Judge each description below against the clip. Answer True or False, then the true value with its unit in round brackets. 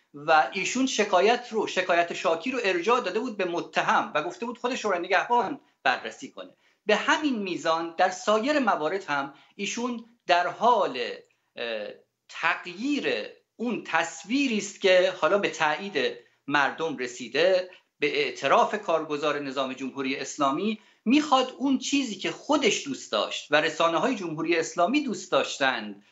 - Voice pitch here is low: False (190 Hz)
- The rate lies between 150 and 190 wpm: False (140 wpm)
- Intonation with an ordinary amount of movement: False (7.8 semitones)